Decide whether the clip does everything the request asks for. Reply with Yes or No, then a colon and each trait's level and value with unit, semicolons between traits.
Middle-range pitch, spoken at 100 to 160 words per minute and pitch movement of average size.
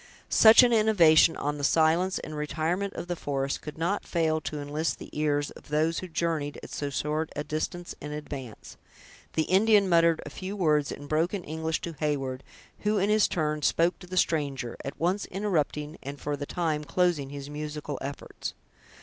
No: medium, 155 Hz; average, 185 wpm; average, 3.1 semitones